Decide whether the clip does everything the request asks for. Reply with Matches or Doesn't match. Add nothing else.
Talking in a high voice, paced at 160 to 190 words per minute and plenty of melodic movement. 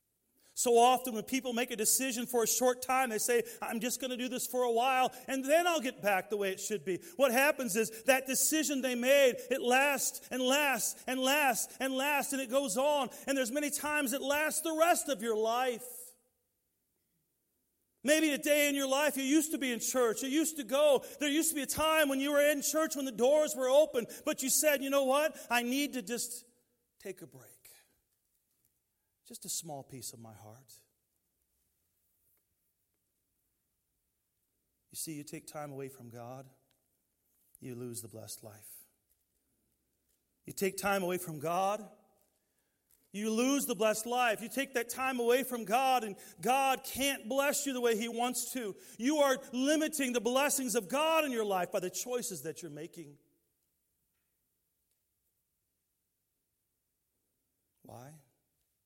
Matches